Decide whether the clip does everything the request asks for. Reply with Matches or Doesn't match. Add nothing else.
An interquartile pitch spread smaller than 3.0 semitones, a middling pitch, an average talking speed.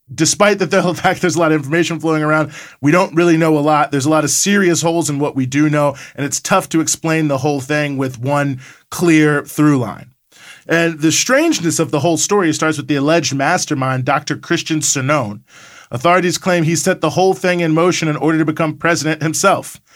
Doesn't match